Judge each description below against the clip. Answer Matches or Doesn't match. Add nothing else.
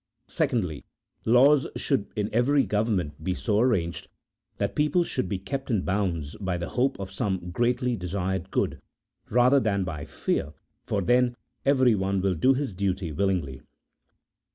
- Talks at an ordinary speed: Matches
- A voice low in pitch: Matches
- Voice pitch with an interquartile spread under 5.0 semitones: Doesn't match